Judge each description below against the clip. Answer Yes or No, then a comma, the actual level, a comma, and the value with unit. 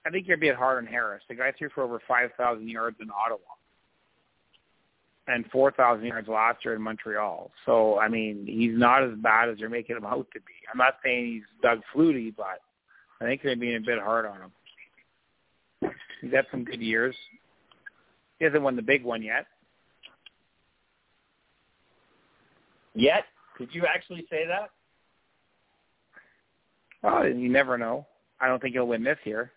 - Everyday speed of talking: Yes, average, 175 wpm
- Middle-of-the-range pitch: No, low, 120 Hz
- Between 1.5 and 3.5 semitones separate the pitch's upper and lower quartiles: Yes, average, 2.9 semitones